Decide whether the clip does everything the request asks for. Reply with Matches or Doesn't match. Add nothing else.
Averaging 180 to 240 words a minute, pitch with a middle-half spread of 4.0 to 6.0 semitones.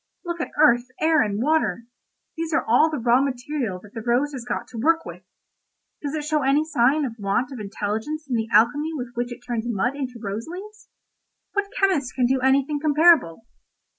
Matches